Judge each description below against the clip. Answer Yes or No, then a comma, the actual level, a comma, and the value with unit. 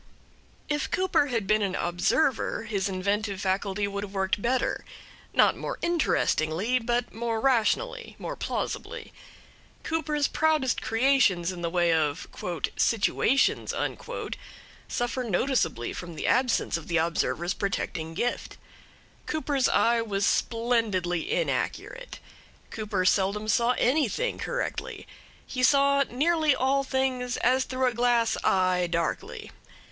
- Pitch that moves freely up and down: Yes, wide, 5.7 semitones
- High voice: Yes, high, 230 Hz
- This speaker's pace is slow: Yes, slow, 120 wpm